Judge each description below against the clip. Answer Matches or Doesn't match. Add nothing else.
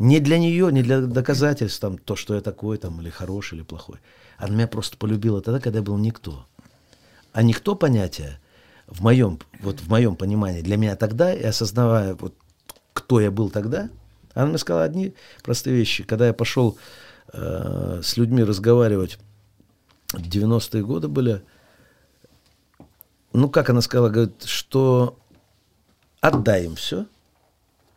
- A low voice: Matches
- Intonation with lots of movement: Doesn't match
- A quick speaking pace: Doesn't match